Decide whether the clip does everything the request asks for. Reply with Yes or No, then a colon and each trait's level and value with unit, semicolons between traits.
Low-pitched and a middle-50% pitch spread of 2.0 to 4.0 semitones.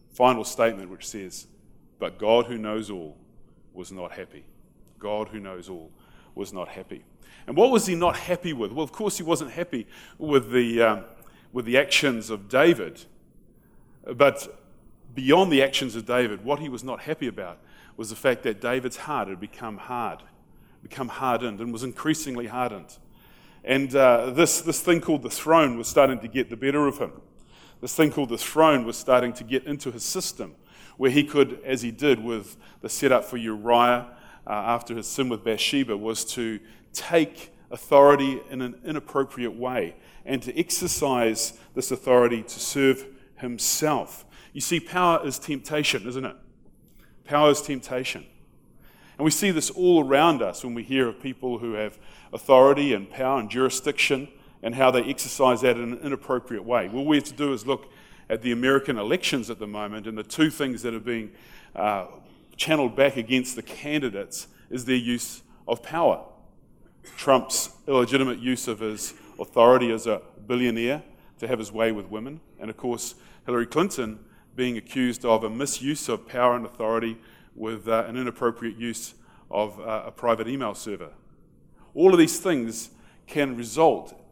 Yes: low, 125 Hz; average, 3.4 semitones